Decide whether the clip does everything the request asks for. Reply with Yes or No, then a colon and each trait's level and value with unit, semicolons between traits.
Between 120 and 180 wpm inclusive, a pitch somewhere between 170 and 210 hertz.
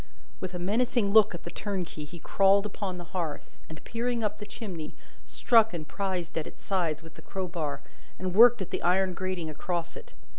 No: average, 195 wpm; medium, 185 Hz